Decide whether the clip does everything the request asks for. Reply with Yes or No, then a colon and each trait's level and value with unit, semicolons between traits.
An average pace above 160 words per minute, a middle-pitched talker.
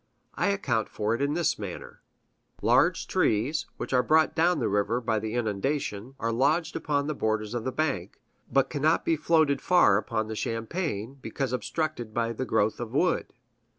No: average, 180 wpm; low, 125 Hz